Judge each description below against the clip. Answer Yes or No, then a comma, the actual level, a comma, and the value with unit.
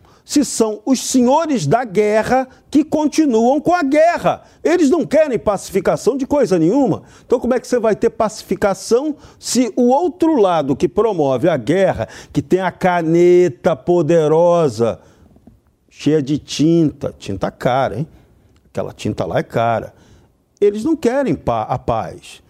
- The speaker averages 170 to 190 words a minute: No, average, 145 wpm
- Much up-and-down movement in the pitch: Yes, wide, 8.1 semitones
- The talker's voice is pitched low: No, high, 215 Hz